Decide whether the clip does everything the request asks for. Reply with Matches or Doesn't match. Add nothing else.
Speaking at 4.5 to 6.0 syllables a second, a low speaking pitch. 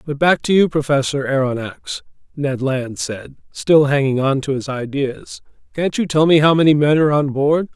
Doesn't match